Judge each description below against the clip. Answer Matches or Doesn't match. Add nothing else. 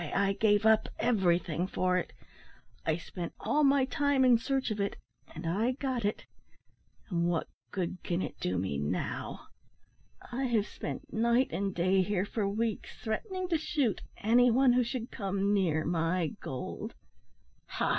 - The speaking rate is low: Doesn't match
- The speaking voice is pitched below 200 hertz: Doesn't match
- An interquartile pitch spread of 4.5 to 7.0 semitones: Matches